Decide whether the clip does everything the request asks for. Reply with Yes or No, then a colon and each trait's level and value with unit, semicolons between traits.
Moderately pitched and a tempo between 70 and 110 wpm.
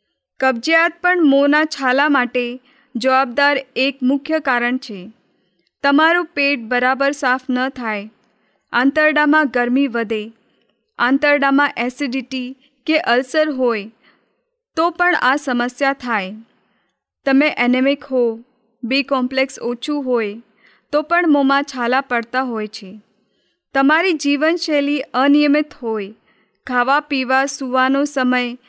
No: very high, 260 Hz; average, 105 wpm